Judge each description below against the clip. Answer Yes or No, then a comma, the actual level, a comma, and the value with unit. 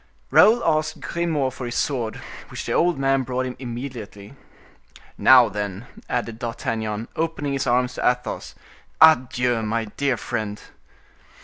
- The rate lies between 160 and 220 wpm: No, slow, 135 wpm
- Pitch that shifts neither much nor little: Yes, average, 3.2 semitones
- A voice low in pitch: Yes, low, 125 Hz